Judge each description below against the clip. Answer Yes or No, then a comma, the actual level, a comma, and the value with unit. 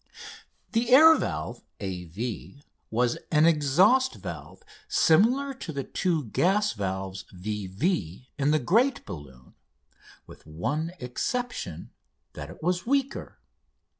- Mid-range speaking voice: Yes, medium, 145 Hz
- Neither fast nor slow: No, slow, 120 wpm